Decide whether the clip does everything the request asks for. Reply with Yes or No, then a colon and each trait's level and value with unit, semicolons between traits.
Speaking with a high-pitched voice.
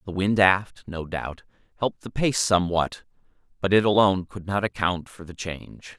No: very low, 95 Hz